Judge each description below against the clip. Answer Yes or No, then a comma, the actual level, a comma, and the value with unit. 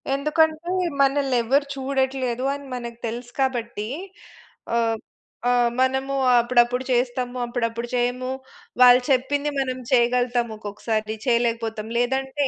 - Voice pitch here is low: No, very high, 250 Hz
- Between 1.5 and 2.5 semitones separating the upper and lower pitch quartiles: Yes, narrow, 2.1 semitones